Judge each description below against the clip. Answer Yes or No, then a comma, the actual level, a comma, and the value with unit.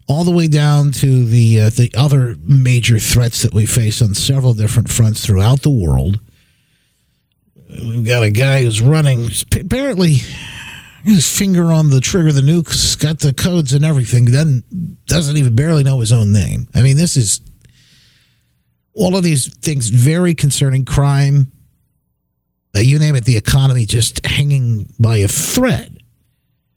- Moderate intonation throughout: Yes, average, 3.9 semitones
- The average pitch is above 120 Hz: Yes, low, 130 Hz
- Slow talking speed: No, average, 160 wpm